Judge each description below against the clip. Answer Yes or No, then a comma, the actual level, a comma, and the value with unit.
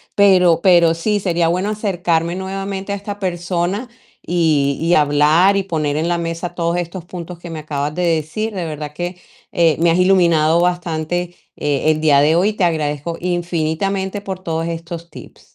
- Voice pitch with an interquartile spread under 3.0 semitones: Yes, narrow, 2.5 semitones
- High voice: No, medium, 170 Hz